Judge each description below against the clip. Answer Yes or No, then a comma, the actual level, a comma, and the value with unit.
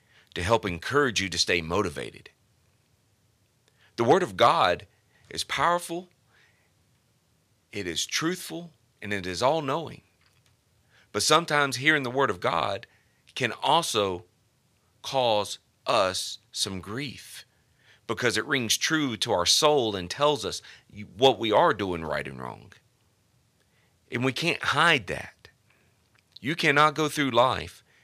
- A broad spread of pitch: Yes, wide, 5.7 semitones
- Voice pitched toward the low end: Yes, low, 120 Hz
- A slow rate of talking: Yes, slow, 130 wpm